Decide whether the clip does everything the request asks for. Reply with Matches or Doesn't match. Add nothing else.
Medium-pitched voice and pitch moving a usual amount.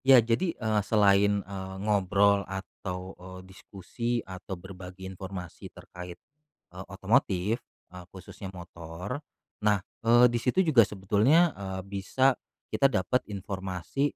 Doesn't match